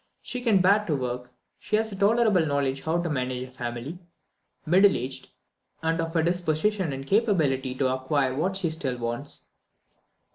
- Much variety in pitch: Yes, wide, 6.5 semitones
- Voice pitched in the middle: Yes, medium, 155 Hz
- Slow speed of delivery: No, average, 170 wpm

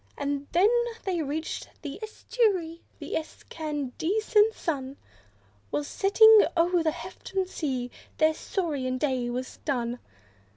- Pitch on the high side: Yes, very high, 315 Hz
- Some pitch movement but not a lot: No, wide, 5.9 semitones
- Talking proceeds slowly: Yes, slow, 115 wpm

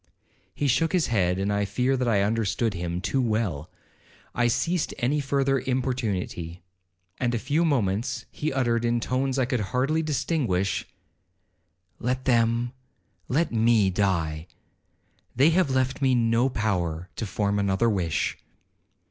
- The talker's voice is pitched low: Yes, low, 120 Hz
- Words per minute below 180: Yes, average, 140 wpm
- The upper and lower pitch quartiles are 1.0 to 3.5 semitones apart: No, average, 5.0 semitones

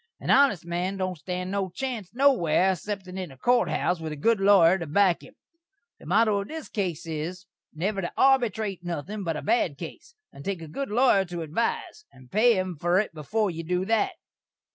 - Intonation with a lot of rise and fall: No, average, 4.5 semitones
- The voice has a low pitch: No, high, 190 Hz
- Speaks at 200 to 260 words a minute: Yes, fast, 205 wpm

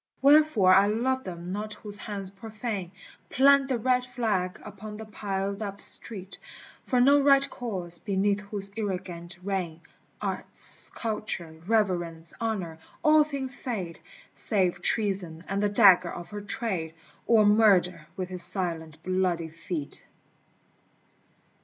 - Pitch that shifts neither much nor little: Yes, average, 3.8 semitones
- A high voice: Yes, high, 200 Hz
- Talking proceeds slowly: Yes, slow, 130 wpm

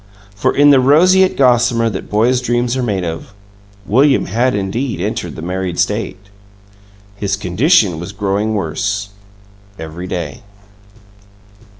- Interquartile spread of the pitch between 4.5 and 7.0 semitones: Yes, average, 5.1 semitones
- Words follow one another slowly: Yes, slow, 125 wpm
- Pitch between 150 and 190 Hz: No, low, 105 Hz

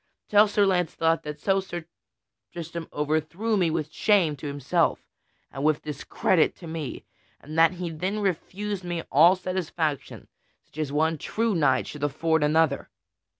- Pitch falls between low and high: Yes, medium, 165 Hz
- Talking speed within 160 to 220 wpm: No, average, 150 wpm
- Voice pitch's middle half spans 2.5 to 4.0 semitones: Yes, average, 3.4 semitones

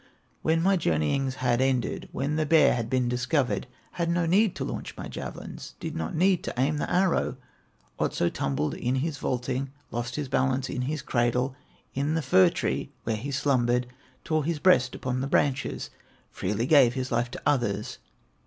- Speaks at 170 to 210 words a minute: Yes, average, 180 wpm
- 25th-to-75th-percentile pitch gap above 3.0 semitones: Yes, average, 3.7 semitones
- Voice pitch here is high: No, low, 130 Hz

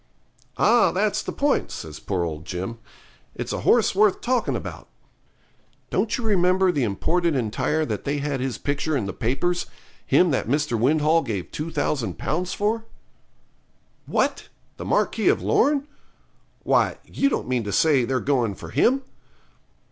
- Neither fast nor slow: Yes, average, 155 wpm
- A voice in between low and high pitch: Yes, medium, 150 Hz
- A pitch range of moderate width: No, wide, 7.7 semitones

